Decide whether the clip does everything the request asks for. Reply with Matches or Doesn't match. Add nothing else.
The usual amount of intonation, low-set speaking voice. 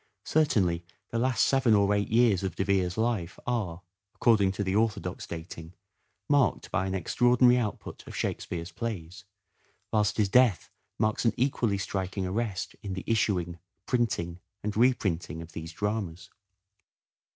Matches